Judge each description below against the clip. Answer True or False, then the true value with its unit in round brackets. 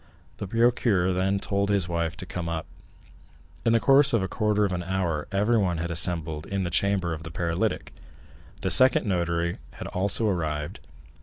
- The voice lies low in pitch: True (90 Hz)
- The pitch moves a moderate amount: True (3.2 semitones)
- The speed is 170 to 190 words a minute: True (175 wpm)